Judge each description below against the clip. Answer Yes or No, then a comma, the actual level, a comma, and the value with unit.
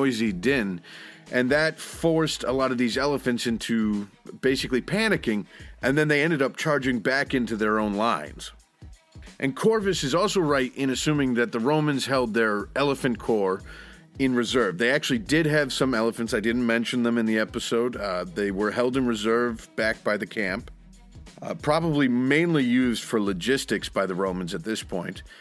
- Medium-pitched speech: No, low, 125 Hz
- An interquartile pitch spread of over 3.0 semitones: Yes, average, 3.9 semitones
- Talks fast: No, average, 175 wpm